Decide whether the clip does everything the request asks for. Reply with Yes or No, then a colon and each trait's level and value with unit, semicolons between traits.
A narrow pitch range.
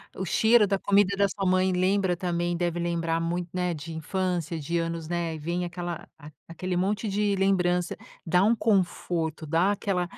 Yes: narrow, 2.3 semitones